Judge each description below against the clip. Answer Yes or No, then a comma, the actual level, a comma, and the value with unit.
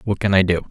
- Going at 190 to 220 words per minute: No, fast, 340 wpm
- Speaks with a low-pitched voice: Yes, very low, 95 Hz